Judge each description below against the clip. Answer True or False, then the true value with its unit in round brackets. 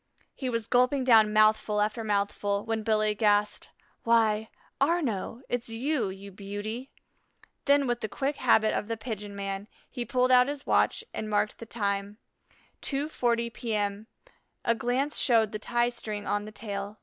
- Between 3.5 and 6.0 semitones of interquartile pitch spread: False (2.8 semitones)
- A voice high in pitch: True (220 Hz)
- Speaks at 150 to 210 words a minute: True (160 wpm)